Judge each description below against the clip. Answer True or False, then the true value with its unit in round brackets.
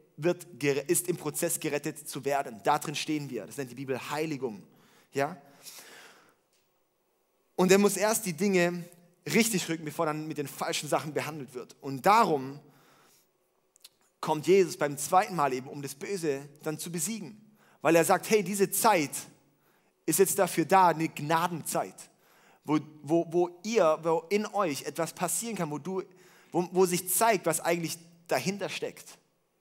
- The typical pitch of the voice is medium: True (170 Hz)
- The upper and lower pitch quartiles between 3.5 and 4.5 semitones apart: True (4.0 semitones)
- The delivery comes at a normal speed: True (160 wpm)